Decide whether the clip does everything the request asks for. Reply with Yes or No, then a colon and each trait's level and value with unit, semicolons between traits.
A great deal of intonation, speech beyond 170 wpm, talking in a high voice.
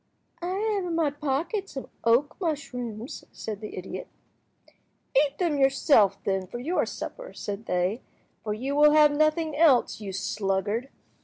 No: wide, 6.3 semitones; average, 150 wpm; very high, 275 Hz